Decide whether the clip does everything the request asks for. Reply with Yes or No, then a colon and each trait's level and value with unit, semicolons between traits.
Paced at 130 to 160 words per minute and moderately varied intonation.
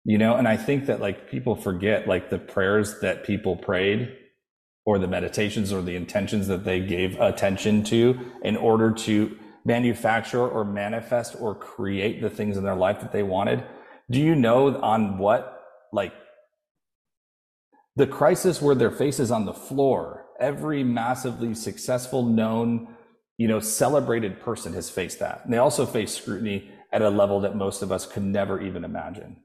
No: average, 170 wpm; average, 3.5 semitones